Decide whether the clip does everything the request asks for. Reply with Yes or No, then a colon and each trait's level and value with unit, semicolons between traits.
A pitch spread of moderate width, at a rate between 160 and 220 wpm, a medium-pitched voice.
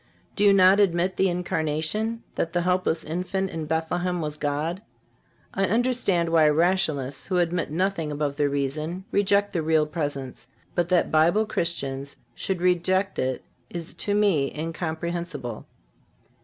No: average, 3.5 semitones; average, 140 wpm; medium, 170 Hz